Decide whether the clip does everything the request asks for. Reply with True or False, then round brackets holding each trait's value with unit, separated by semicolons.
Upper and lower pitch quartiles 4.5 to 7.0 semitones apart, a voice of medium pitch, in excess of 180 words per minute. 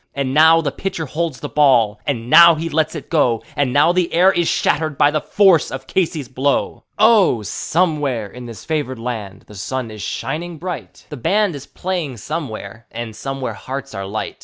True (5.5 semitones; 145 Hz; 190 wpm)